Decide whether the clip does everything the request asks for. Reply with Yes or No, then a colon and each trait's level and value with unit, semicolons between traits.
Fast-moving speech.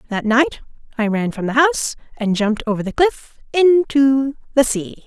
No: average, 180 wpm